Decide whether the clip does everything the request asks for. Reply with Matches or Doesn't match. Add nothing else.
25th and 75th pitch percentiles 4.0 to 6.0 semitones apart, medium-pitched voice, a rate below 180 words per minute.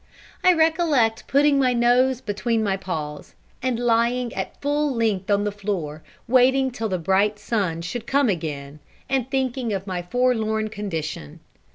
Doesn't match